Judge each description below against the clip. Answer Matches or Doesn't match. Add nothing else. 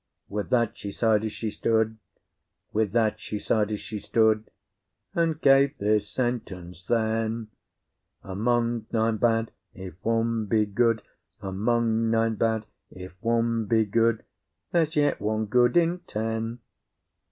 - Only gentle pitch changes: Matches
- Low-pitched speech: Matches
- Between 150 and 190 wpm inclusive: Doesn't match